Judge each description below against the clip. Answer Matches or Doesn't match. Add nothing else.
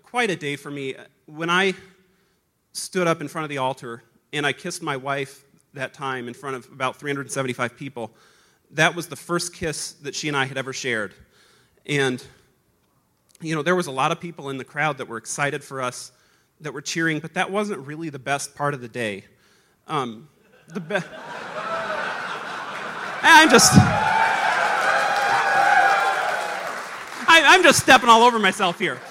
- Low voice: Doesn't match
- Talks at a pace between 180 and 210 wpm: Doesn't match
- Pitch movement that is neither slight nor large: Matches